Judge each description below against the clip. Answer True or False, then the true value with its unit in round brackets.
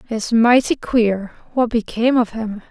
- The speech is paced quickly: False (155 wpm)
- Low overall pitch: False (230 Hz)